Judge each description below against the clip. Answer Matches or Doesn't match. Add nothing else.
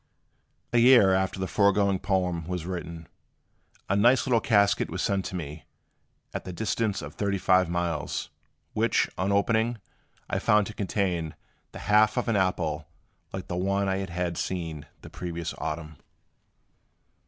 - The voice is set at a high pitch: Doesn't match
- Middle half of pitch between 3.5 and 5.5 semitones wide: Doesn't match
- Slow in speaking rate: Doesn't match